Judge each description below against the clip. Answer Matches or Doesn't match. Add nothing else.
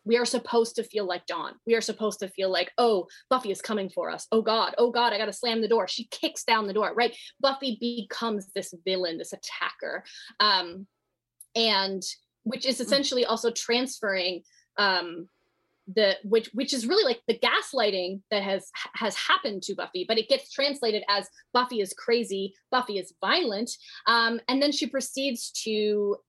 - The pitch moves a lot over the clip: Doesn't match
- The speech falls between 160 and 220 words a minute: Matches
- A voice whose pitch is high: Matches